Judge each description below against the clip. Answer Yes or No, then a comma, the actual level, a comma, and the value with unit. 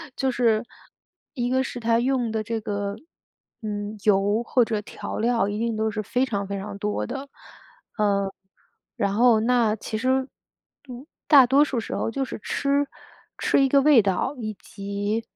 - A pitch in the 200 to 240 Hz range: Yes, high, 225 Hz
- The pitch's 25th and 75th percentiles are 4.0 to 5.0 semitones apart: No, average, 3.6 semitones